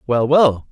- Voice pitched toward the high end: No, low, 130 Hz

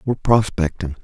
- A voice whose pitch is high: No, very low, 95 Hz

